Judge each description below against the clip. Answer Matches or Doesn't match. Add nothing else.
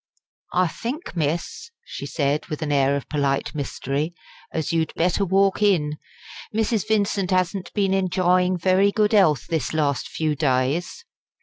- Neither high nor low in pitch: Matches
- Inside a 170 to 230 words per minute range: Doesn't match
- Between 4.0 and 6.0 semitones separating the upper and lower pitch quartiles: Matches